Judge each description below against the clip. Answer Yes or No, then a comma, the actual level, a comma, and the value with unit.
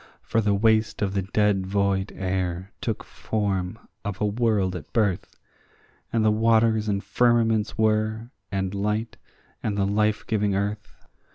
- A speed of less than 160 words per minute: Yes, average, 150 wpm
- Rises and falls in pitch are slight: Yes, narrow, 2.0 semitones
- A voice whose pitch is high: No, low, 105 Hz